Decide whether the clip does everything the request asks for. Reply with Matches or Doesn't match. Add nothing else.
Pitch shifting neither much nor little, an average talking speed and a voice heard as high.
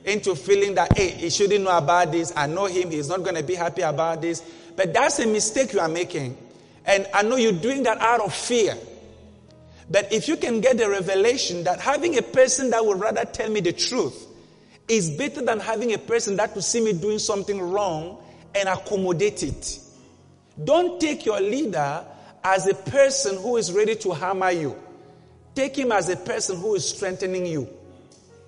Matches